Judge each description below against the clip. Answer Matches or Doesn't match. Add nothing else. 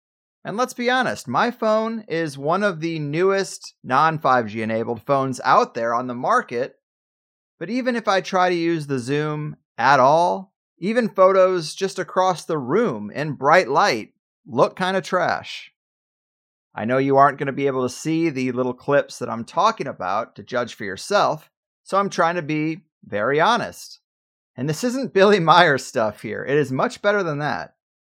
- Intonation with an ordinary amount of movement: Doesn't match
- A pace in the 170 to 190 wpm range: Matches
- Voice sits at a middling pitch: Matches